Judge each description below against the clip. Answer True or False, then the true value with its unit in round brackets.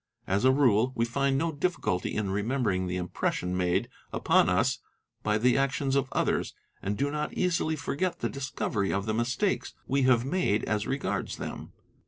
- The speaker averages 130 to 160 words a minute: False (170 wpm)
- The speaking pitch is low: True (125 Hz)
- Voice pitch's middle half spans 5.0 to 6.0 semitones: True (5.4 semitones)